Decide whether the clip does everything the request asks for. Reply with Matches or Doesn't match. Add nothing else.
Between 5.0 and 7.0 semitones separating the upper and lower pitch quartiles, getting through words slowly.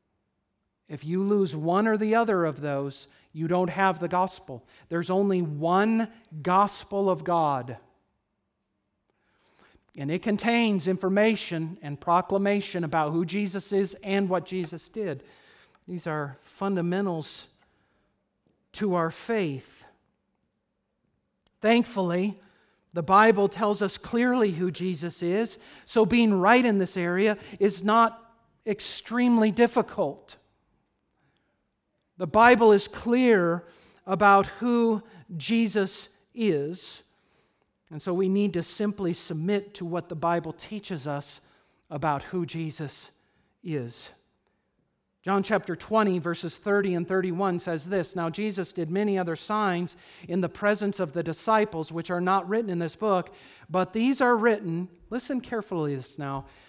Doesn't match